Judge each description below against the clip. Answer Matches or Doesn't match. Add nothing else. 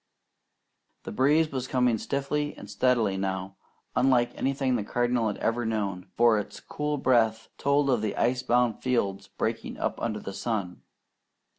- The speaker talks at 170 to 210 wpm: Doesn't match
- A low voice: Matches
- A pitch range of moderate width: Matches